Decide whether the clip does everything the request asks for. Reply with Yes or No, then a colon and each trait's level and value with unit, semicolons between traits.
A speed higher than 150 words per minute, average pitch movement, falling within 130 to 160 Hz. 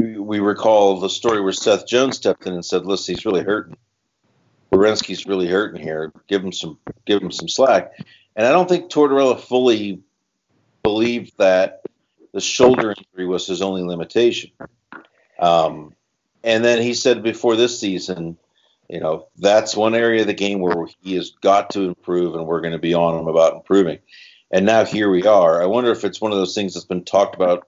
No: average, 195 wpm; average, 3.9 semitones; very low, 95 Hz